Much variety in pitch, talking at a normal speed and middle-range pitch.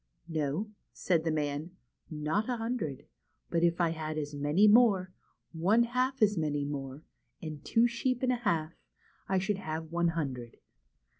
Yes: wide, 5.7 semitones; average, 170 wpm; medium, 170 Hz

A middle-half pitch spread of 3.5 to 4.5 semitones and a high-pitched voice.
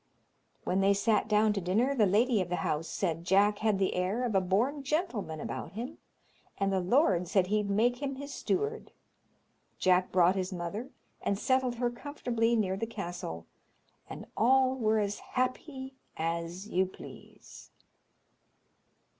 No: average, 5.0 semitones; high, 210 Hz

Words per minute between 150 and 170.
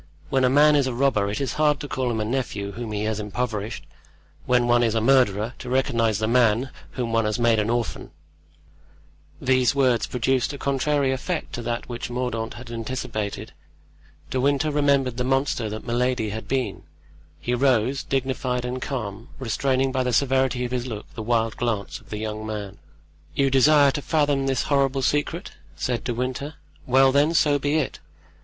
No: average, 185 wpm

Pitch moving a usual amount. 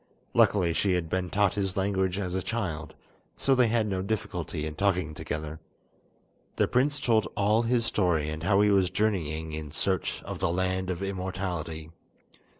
Yes: average, 4.0 semitones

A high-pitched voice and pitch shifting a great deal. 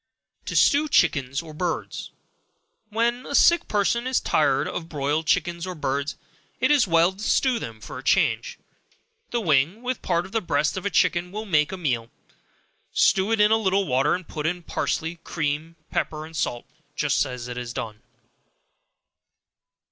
No: medium, 170 Hz; wide, 6.1 semitones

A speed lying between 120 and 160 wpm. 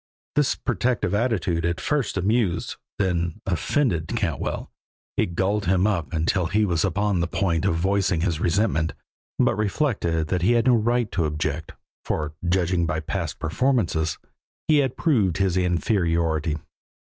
Yes: average, 145 wpm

